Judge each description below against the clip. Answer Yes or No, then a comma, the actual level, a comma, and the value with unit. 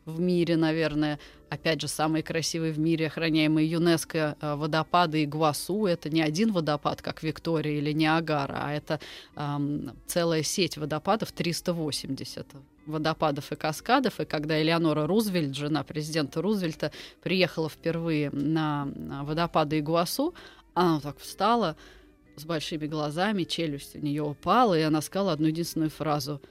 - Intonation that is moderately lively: No, narrow, 1.9 semitones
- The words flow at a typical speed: Yes, average, 140 wpm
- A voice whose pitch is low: No, medium, 155 Hz